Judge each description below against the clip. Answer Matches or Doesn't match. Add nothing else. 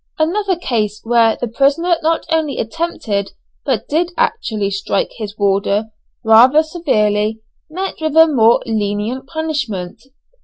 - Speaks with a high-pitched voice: Matches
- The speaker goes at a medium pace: Doesn't match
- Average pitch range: Doesn't match